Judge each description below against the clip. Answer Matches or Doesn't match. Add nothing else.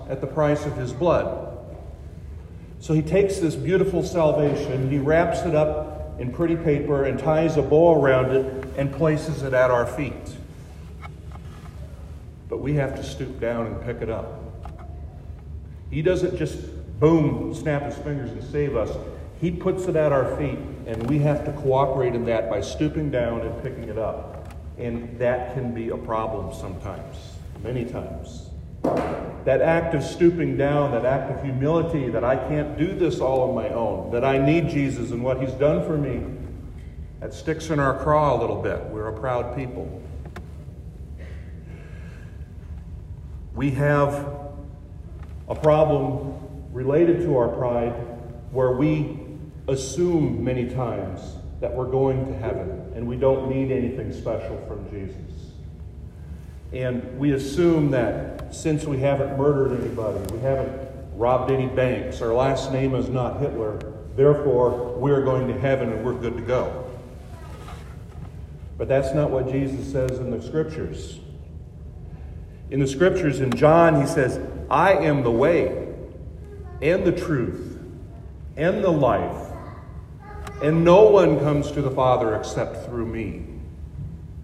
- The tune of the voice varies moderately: Doesn't match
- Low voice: Matches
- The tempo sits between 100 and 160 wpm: Matches